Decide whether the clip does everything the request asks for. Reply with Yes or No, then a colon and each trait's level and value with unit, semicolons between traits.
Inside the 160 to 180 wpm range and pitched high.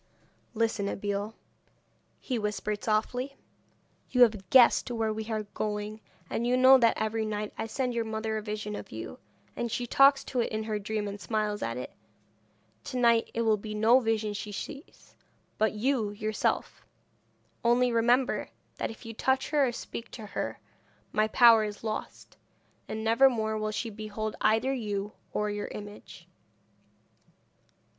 Yes: average, 165 wpm; high, 220 Hz